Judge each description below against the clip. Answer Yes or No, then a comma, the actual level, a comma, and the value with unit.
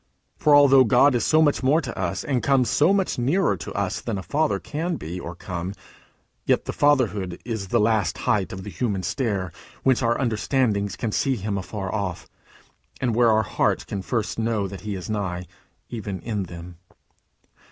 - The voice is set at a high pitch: No, low, 110 Hz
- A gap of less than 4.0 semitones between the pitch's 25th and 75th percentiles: No, average, 5.3 semitones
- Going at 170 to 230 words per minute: Yes, average, 190 wpm